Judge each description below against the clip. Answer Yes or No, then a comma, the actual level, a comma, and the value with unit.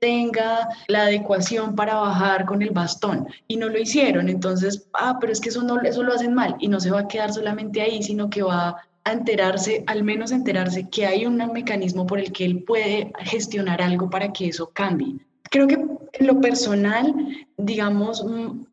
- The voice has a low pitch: No, high, 215 Hz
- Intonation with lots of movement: No, average, 3.0 semitones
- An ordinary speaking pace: Yes, average, 190 wpm